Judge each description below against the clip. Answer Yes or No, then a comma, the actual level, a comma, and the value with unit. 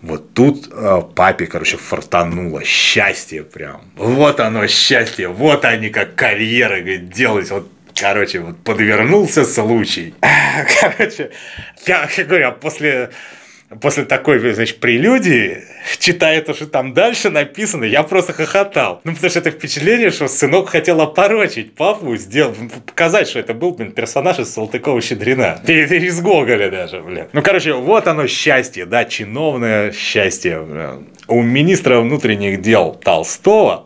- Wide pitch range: Yes, wide, 6.4 semitones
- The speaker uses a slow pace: No, average, 140 wpm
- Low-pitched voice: No, medium, 145 Hz